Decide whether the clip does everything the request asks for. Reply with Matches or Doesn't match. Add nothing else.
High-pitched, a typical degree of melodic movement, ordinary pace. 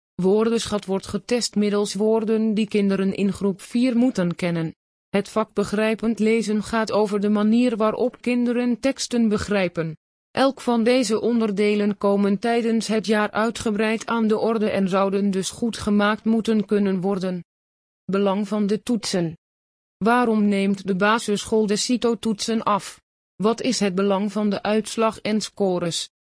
Doesn't match